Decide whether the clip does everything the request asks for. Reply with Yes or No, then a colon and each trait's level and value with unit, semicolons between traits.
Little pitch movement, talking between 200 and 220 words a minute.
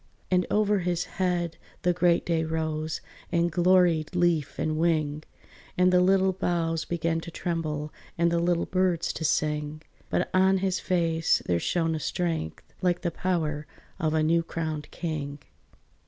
No: narrow, 2.2 semitones; average, 155 wpm